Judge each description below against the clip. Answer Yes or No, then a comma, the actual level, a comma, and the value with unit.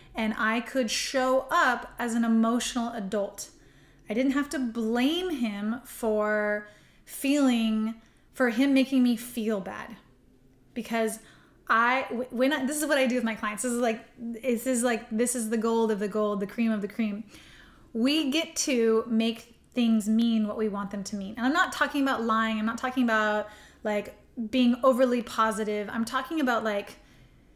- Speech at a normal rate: Yes, average, 180 wpm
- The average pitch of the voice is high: Yes, high, 230 Hz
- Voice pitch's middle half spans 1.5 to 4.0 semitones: Yes, average, 2.8 semitones